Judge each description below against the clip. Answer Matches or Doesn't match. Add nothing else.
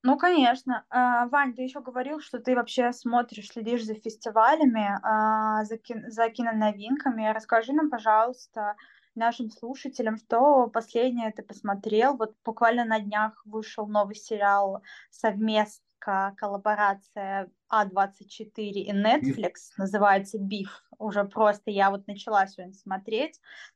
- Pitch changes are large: Doesn't match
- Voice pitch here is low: Doesn't match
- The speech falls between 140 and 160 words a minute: Doesn't match